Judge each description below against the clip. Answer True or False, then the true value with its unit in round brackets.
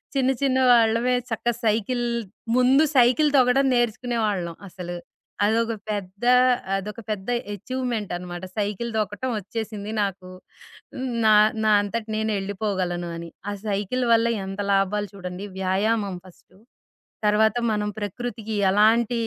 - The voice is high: True (210 Hz)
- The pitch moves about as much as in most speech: True (3.3 semitones)